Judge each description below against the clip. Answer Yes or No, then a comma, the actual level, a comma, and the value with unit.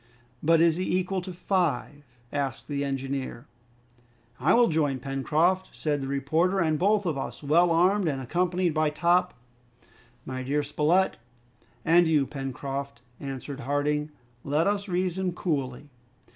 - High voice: No, medium, 150 Hz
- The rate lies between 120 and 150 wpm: Yes, average, 145 wpm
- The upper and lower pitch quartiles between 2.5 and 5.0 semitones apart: Yes, average, 4.4 semitones